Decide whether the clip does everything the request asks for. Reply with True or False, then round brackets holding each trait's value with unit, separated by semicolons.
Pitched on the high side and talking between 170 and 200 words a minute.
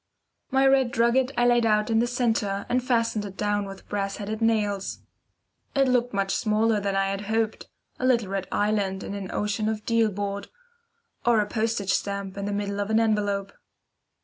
True (210 Hz; 190 wpm)